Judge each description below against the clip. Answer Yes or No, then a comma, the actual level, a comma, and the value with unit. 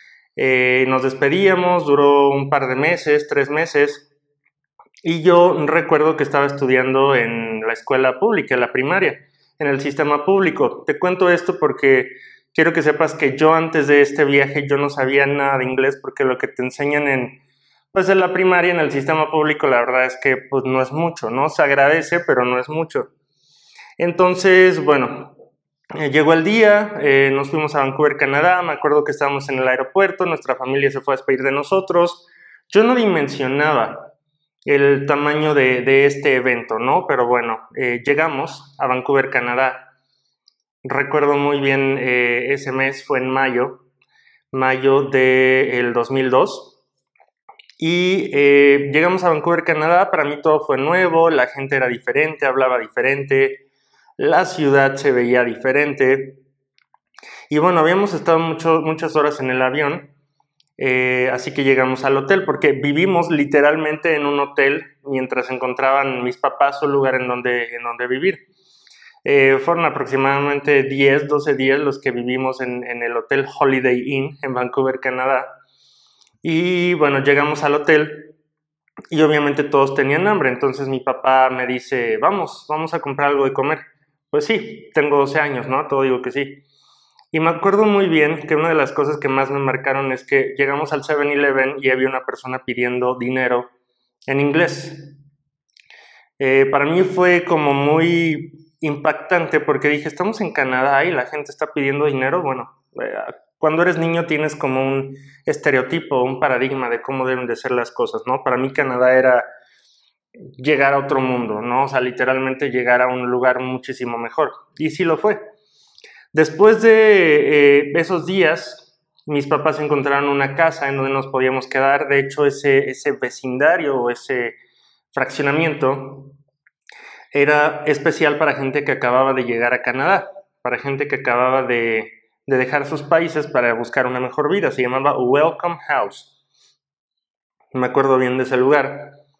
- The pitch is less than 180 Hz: Yes, medium, 140 Hz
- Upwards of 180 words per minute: No, average, 165 wpm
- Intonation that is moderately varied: Yes, average, 3.0 semitones